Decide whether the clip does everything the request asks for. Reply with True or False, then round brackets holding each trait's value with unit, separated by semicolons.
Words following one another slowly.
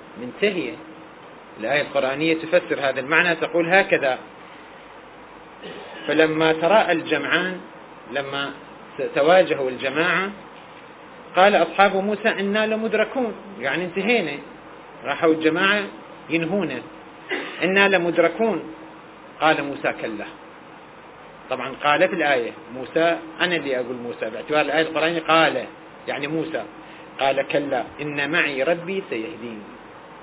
False (95 wpm)